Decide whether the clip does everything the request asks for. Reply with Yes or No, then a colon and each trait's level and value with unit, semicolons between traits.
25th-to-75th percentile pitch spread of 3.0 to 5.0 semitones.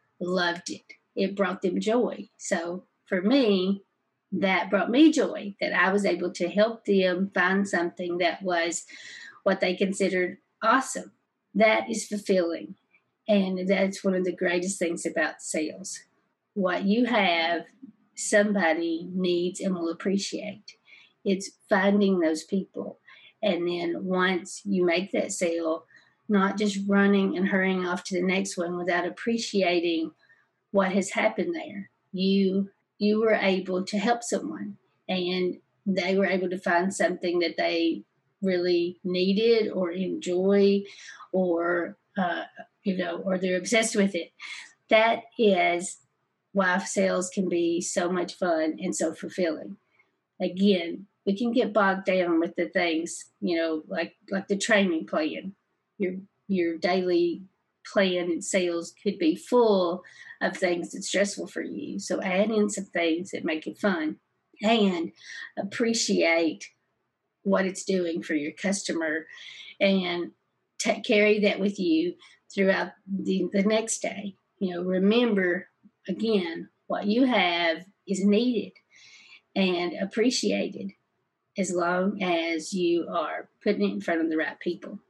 No: narrow, 2.5 semitones